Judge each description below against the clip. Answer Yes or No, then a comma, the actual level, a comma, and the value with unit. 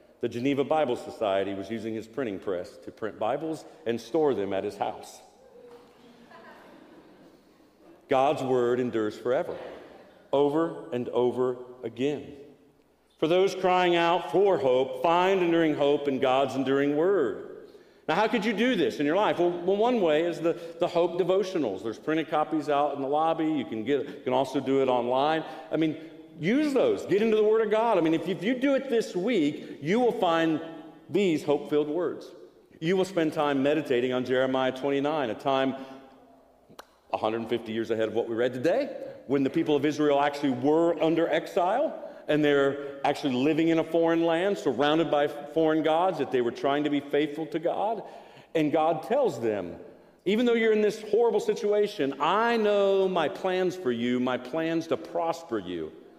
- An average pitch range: No, wide, 6.0 semitones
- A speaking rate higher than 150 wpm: Yes, average, 180 wpm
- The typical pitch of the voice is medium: Yes, medium, 160 Hz